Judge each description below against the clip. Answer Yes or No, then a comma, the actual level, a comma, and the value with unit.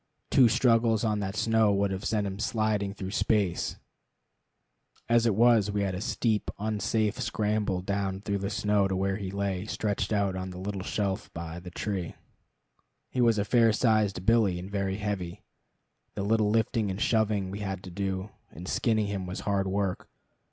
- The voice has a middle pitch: No, low, 100 Hz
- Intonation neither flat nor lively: No, narrow, 2.1 semitones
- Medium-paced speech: Yes, average, 180 wpm